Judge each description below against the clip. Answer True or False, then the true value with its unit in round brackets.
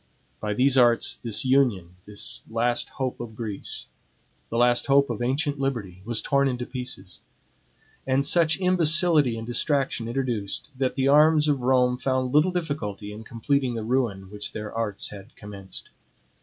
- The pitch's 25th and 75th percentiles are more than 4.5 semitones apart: False (4.1 semitones)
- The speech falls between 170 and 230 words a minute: False (155 wpm)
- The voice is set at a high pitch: False (125 Hz)